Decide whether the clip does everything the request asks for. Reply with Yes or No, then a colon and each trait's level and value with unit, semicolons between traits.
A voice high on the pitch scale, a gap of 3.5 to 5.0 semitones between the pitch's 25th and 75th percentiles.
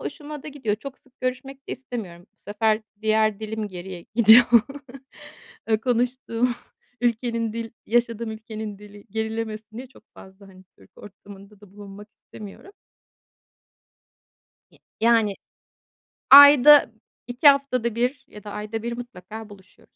No: high, 220 Hz; average, 2.9 semitones